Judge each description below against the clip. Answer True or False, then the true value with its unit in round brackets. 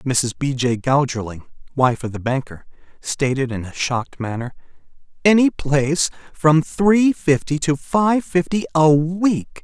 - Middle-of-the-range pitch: True (145 Hz)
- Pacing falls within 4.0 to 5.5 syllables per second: True (4.2 syllables/s)